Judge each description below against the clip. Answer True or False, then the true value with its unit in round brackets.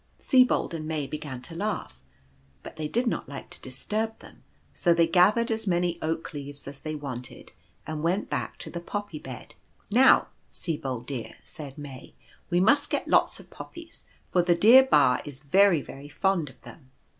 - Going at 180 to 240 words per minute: True (190 wpm)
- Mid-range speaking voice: True (165 Hz)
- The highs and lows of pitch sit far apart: True (6.0 semitones)